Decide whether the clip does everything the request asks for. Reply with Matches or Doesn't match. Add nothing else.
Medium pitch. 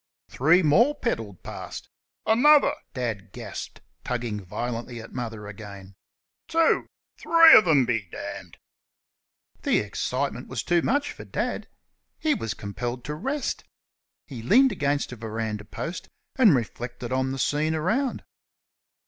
Doesn't match